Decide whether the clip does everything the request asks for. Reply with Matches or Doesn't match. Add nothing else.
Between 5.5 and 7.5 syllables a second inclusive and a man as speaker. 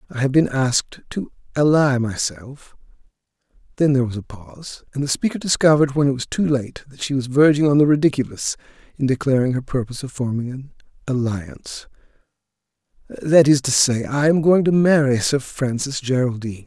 Matches